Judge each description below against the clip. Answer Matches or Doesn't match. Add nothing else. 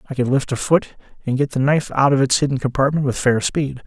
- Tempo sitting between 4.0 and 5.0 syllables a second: Doesn't match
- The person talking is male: Matches